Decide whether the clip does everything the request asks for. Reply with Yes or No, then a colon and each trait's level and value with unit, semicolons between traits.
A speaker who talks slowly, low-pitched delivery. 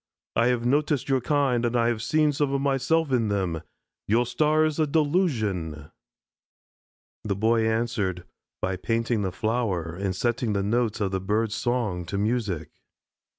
No: average, 160 wpm; low, 115 Hz